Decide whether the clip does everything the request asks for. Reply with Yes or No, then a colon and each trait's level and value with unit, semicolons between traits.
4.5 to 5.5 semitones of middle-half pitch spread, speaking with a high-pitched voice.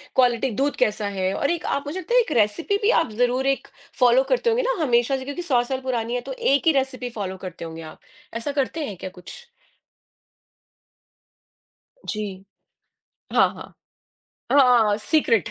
Yes: average, 5.1 semitones; very high, 250 Hz